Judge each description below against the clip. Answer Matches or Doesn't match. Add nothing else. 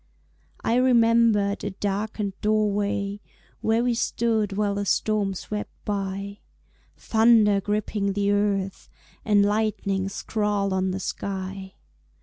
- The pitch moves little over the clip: Matches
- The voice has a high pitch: Matches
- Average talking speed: Doesn't match